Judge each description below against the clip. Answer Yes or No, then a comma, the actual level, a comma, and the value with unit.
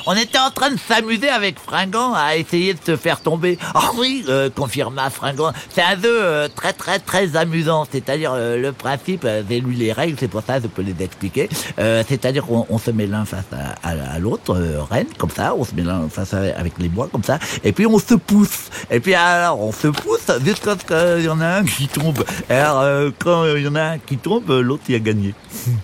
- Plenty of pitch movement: Yes, wide, 7.0 semitones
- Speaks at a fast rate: Yes, fast, 245 wpm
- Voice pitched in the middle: Yes, medium, 145 Hz